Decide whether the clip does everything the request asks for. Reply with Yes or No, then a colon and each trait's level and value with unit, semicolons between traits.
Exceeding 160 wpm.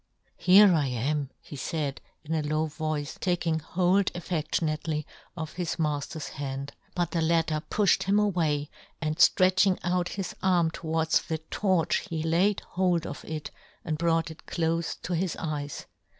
Yes: average, 170 wpm